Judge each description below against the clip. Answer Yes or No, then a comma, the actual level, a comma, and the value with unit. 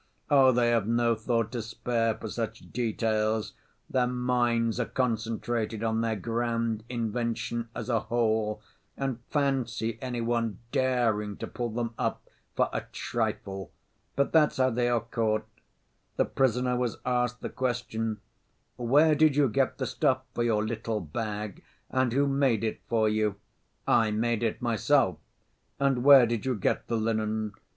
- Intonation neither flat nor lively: No, narrow, 2.1 semitones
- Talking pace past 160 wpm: No, average, 155 wpm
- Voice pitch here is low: Yes, low, 115 Hz